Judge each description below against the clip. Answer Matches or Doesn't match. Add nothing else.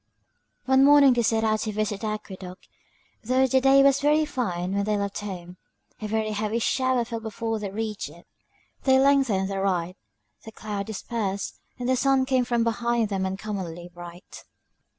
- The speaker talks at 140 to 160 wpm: Doesn't match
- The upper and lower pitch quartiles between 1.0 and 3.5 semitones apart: Doesn't match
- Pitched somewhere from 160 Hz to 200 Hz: Doesn't match